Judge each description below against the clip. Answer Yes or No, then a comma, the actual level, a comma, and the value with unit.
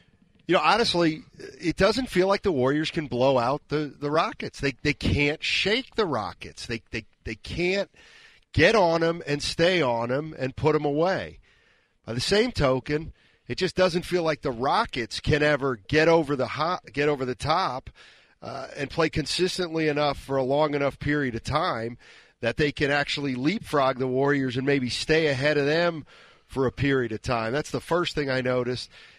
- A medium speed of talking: Yes, average, 190 wpm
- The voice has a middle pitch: Yes, medium, 145 Hz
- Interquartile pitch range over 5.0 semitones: No, average, 3.8 semitones